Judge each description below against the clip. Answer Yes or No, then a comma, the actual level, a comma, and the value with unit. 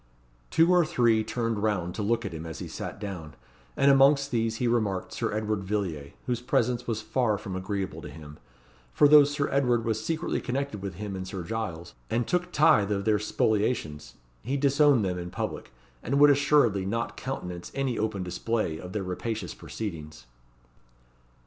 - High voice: No, low, 110 Hz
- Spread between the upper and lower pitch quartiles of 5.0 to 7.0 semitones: Yes, average, 5.3 semitones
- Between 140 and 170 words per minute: No, average, 180 wpm